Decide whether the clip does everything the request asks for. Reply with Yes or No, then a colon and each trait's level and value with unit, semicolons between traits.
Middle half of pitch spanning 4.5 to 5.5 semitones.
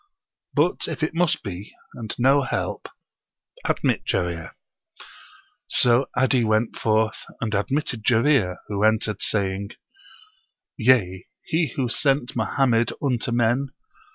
No: average, 3.8 semitones